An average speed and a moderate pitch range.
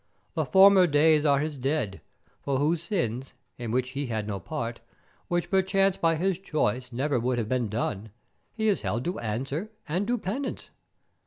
No: average, 175 wpm; wide, 7.1 semitones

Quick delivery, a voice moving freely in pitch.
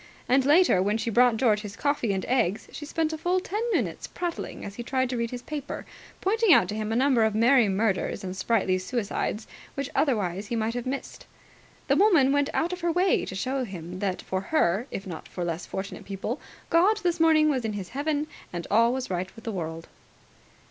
Yes: fast, 215 wpm; wide, 6.6 semitones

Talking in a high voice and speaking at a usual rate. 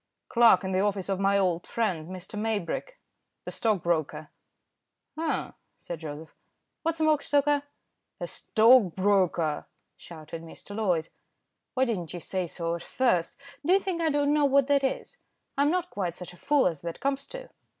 Yes: high, 200 Hz; average, 165 wpm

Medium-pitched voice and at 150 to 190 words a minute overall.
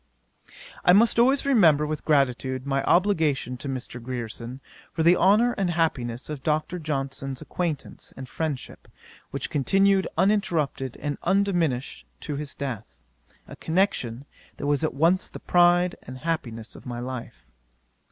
No: medium, 150 Hz; average, 140 wpm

